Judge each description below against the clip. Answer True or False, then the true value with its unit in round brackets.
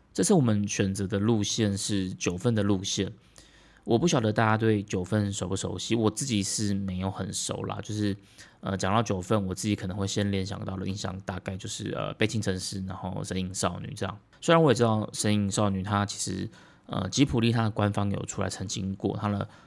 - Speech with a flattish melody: True (2.3 semitones)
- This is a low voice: True (100 Hz)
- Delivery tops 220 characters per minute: True (315 characters per minute)